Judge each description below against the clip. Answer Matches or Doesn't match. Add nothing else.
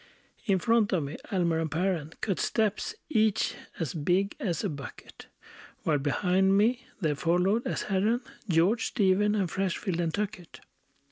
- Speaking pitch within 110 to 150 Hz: Doesn't match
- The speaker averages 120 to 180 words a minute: Matches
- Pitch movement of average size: Matches